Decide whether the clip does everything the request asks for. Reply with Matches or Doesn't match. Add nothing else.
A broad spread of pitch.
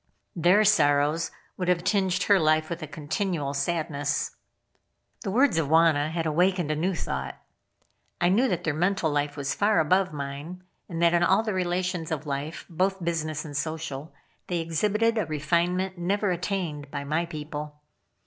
Doesn't match